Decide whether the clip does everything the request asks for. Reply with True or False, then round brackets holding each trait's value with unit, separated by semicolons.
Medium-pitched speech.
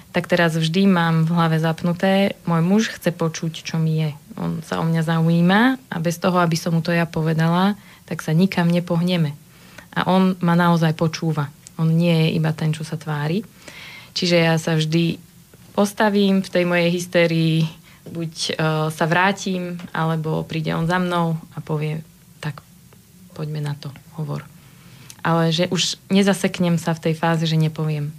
True (165 Hz)